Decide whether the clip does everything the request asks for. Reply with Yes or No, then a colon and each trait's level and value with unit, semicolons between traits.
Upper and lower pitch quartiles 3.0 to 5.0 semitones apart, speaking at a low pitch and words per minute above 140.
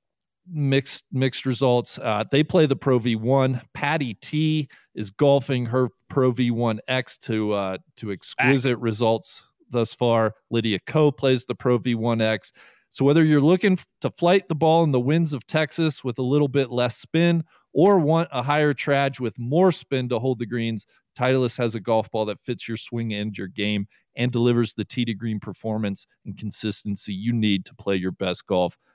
Yes: average, 4.1 semitones; low, 125 Hz; average, 180 wpm